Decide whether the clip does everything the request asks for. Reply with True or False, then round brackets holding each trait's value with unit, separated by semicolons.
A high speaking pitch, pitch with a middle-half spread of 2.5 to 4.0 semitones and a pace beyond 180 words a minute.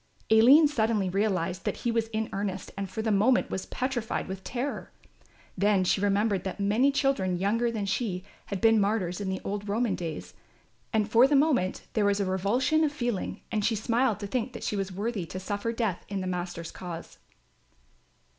True (205 Hz; 3.6 semitones; 195 wpm)